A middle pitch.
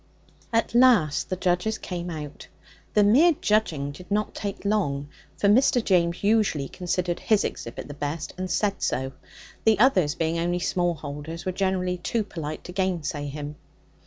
Yes: medium, 180 Hz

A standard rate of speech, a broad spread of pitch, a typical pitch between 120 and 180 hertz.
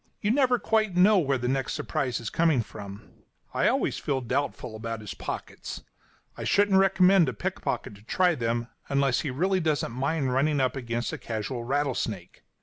Yes: average, 170 wpm; wide, 7.1 semitones; low, 135 Hz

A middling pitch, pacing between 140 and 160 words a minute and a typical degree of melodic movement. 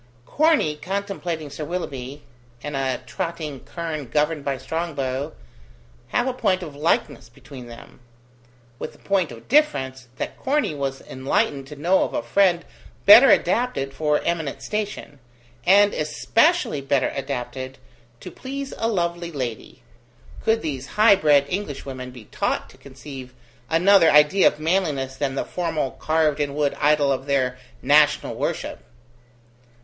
Yes: medium, 150 Hz; average, 145 wpm; average, 4.9 semitones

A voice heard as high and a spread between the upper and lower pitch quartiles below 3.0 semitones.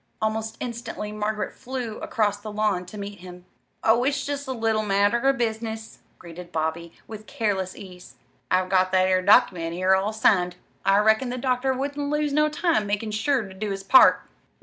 No: high, 215 Hz; average, 4.3 semitones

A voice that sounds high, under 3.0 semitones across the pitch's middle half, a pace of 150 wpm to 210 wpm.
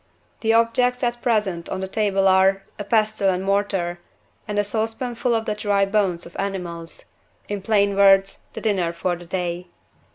Yes: high, 200 Hz; narrow, 2.5 semitones; average, 170 wpm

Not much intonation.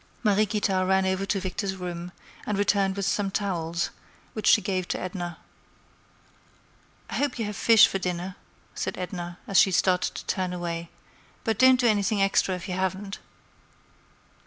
Yes: narrow, 2.1 semitones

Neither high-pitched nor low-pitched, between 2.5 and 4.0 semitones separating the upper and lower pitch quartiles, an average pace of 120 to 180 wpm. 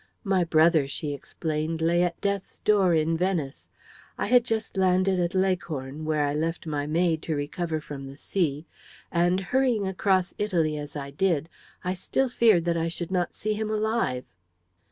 Yes: medium, 170 Hz; average, 3.7 semitones; average, 175 wpm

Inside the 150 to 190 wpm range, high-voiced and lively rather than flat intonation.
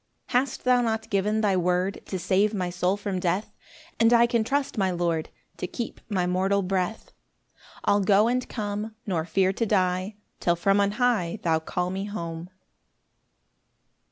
No: average, 170 wpm; high, 195 Hz; average, 3.4 semitones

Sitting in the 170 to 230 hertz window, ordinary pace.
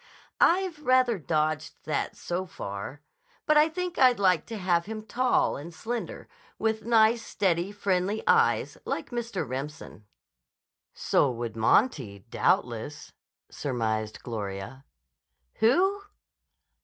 No: medium, 185 Hz; slow, 120 wpm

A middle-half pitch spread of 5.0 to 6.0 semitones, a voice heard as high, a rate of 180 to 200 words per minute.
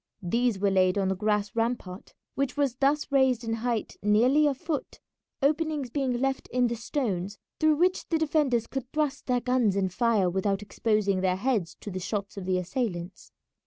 Yes: wide, 5.6 semitones; high, 230 Hz; average, 185 wpm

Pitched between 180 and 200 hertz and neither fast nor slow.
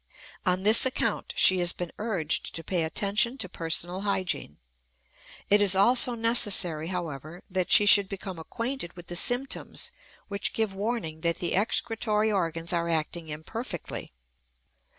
Yes: high, 190 Hz; average, 145 wpm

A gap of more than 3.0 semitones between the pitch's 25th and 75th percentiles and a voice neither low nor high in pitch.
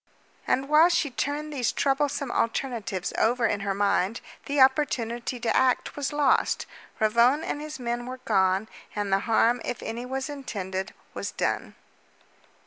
No: average, 4.3 semitones; high, 245 Hz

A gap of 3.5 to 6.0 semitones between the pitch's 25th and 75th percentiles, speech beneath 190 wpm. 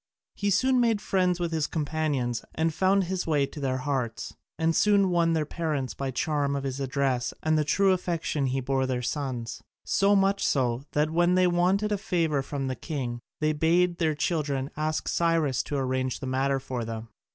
No: average, 4.7 semitones; average, 195 wpm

